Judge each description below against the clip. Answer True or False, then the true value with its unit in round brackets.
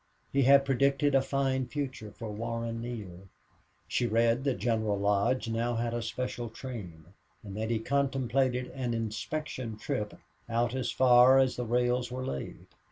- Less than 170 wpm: True (160 wpm)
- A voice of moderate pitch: False (120 Hz)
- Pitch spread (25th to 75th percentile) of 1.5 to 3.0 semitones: True (2.7 semitones)